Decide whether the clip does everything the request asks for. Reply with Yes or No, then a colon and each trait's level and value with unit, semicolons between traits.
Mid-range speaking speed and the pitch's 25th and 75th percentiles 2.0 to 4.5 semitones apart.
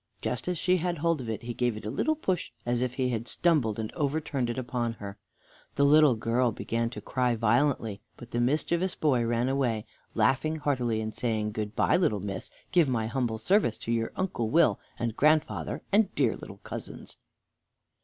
No: average, 195 wpm; average, 4.9 semitones